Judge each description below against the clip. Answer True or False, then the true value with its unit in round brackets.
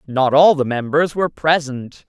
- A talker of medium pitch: True (145 Hz)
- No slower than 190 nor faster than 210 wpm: False (175 wpm)